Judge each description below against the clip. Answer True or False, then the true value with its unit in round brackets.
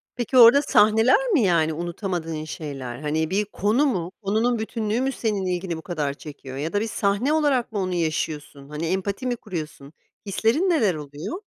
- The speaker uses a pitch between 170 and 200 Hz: True (190 Hz)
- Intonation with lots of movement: True (6.4 semitones)